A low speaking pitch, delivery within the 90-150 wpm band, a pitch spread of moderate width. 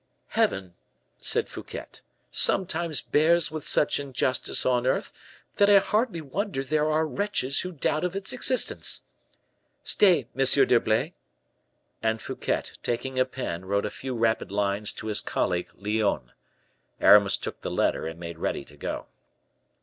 No: low, 130 Hz; average, 145 wpm; wide, 8.0 semitones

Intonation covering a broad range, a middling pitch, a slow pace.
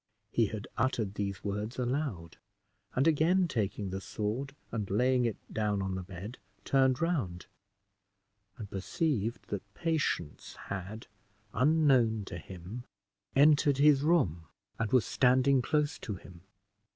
No: wide, 5.7 semitones; low, 115 Hz; slow, 130 wpm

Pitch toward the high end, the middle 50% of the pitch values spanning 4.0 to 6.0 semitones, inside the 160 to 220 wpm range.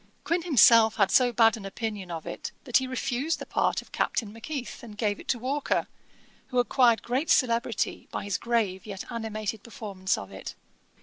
No: high, 230 Hz; average, 3.5 semitones; average, 185 wpm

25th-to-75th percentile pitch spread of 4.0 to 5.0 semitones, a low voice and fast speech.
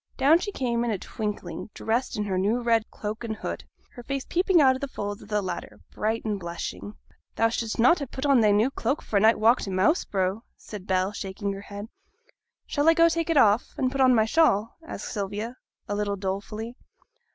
No: average, 4.3 semitones; high, 220 Hz; fast, 220 wpm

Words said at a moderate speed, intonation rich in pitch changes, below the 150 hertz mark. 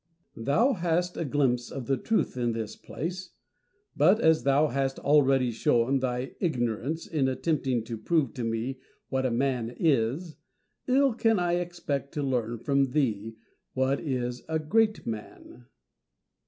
No: average, 155 wpm; average, 4.9 semitones; low, 135 Hz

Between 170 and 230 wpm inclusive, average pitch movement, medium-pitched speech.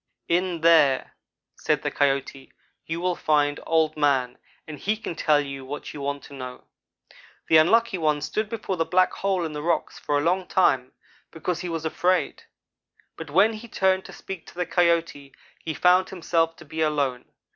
Yes: average, 185 wpm; average, 3.8 semitones; medium, 160 Hz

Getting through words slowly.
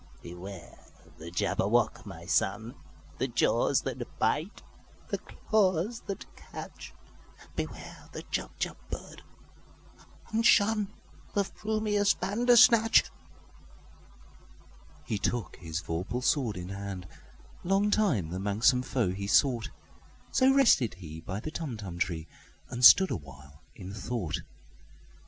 Yes: slow, 95 wpm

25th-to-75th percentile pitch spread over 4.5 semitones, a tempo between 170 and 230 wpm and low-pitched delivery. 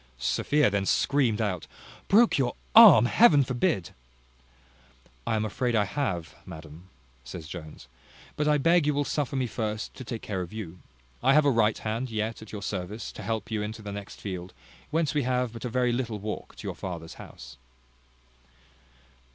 Yes: average, 5.1 semitones; average, 180 wpm; low, 110 Hz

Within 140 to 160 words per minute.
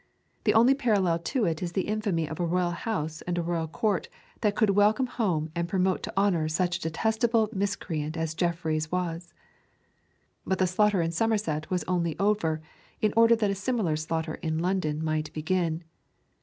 No: average, 180 wpm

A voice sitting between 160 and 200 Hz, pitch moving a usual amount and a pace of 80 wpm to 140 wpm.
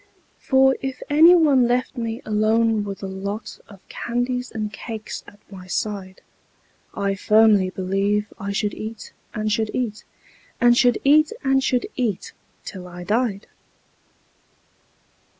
No: high, 215 Hz; average, 3.8 semitones; slow, 135 wpm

